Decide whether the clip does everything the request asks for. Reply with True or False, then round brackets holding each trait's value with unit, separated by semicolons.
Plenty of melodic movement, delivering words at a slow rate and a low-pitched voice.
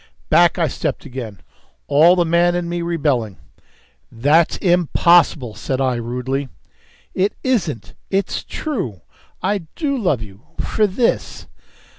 False (6.5 semitones; 125 wpm; 165 Hz)